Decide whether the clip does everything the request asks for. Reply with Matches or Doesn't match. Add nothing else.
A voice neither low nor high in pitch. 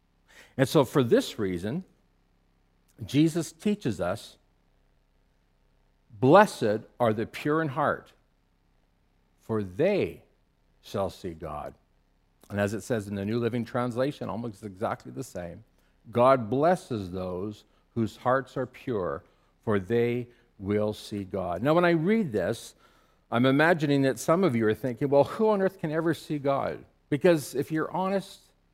Doesn't match